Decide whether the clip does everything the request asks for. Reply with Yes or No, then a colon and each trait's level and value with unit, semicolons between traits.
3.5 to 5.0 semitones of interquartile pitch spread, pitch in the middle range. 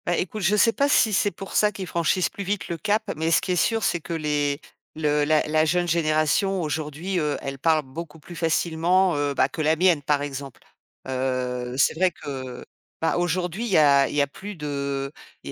Yes: average, 3.9 semitones; medium, 160 Hz